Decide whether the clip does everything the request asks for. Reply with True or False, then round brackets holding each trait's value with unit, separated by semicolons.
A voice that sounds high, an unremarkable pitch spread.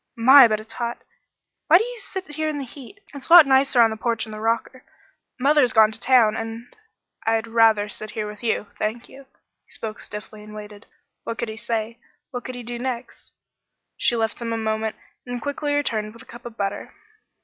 True (230 Hz; 3.1 semitones)